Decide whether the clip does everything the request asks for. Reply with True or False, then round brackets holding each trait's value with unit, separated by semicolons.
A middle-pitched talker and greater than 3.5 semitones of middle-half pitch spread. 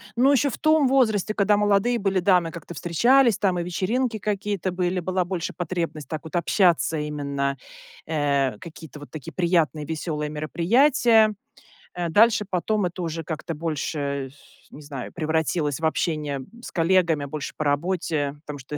True (170 Hz; 4.8 semitones)